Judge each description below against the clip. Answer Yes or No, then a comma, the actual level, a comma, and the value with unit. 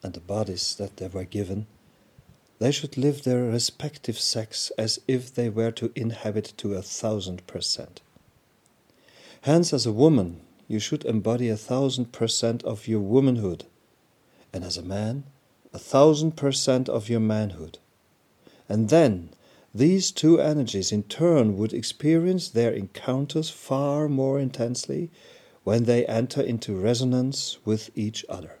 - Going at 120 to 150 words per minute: Yes, average, 145 wpm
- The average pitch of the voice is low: Yes, low, 115 Hz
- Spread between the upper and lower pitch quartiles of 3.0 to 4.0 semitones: No, average, 4.4 semitones